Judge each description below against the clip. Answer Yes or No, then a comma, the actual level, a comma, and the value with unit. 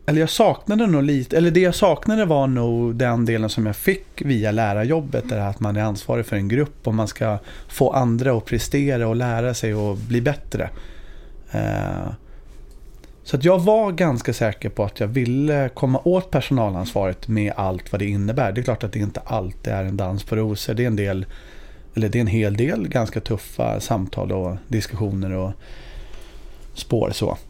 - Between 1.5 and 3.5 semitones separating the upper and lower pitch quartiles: No, average, 4.7 semitones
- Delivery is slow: No, average, 190 wpm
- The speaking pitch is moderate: No, low, 115 Hz